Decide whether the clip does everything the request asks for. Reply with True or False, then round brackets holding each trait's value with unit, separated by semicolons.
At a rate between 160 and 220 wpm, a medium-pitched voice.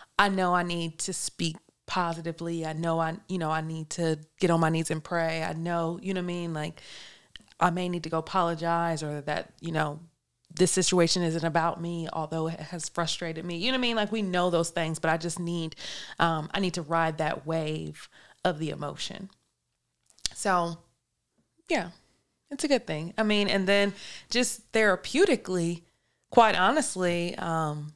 True (190 wpm; 170 Hz)